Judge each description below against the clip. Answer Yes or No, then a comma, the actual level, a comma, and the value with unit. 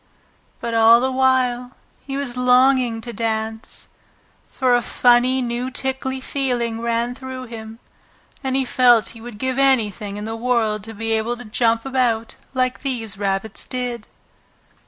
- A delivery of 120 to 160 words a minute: Yes, average, 155 wpm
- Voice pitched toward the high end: Yes, high, 240 Hz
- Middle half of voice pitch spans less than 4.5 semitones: Yes, narrow, 2.4 semitones